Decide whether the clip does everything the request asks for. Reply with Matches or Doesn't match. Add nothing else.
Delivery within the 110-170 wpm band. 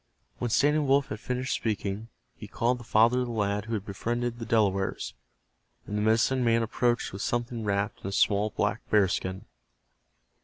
Doesn't match